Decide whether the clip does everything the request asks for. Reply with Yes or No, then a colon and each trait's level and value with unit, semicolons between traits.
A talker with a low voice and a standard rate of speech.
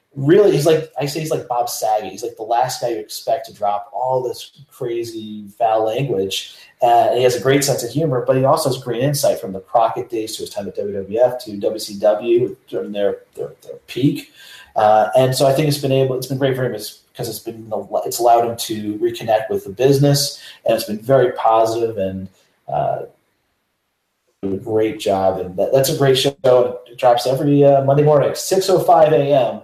No: low, 125 Hz; fast, 210 wpm